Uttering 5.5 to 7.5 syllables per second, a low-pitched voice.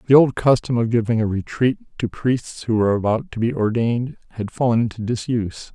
Yes: 5.7 syllables/s; low, 115 Hz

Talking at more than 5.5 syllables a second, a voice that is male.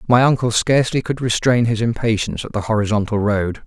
Yes: 6.0 syllables/s; male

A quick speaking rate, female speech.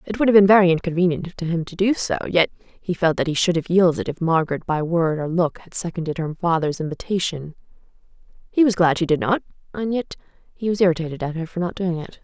Yes: fast, 230 wpm; female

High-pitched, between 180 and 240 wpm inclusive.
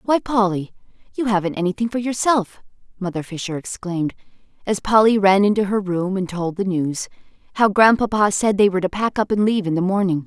Yes: high, 200 Hz; average, 185 wpm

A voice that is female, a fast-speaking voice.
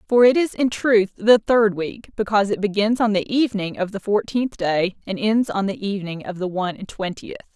Yes: female; fast, 220 wpm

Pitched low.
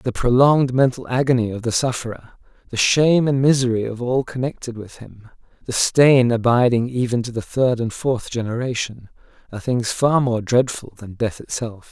Yes: low, 120 Hz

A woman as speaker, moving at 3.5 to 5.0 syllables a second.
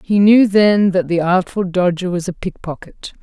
Yes: female; 4.6 syllables/s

